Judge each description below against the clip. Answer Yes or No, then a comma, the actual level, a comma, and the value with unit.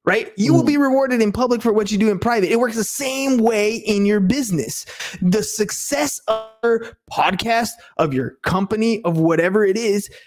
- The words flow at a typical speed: Yes, average, 195 wpm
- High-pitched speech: Yes, high, 220 Hz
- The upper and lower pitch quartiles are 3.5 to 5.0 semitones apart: No, average, 2.9 semitones